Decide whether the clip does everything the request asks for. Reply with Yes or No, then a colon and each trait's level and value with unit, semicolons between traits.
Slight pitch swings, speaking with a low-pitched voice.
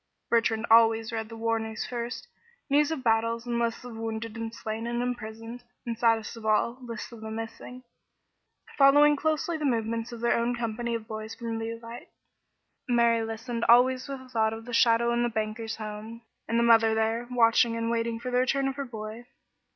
No: narrow, 1.3 semitones; high, 230 Hz